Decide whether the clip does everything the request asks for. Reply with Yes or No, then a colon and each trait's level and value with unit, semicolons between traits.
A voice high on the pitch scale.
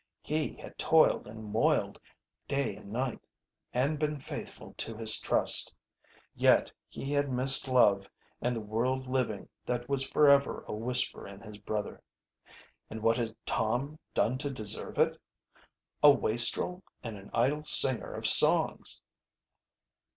No: low, 125 Hz